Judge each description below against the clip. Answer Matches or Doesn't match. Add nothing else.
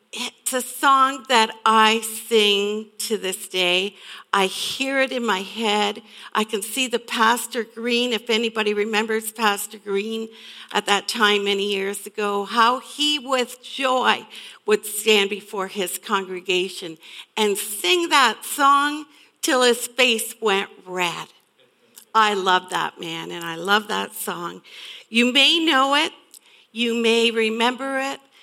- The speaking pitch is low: Doesn't match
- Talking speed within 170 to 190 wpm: Doesn't match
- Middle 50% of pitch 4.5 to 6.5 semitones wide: Doesn't match